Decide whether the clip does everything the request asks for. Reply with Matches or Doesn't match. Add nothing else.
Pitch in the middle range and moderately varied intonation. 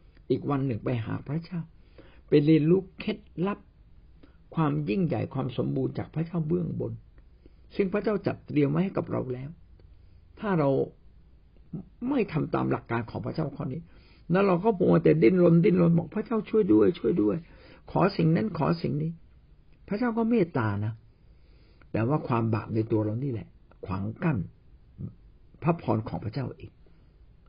Doesn't match